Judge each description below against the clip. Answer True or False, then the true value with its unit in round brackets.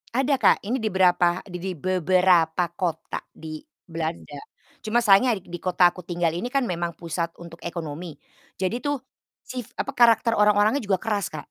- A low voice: False (185 Hz)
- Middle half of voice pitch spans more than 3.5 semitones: True (4.0 semitones)